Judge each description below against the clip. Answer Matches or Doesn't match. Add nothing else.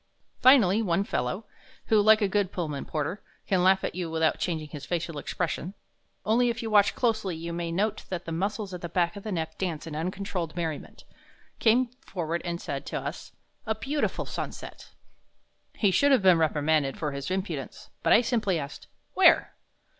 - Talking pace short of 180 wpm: Doesn't match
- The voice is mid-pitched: Matches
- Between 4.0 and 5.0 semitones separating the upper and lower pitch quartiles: Matches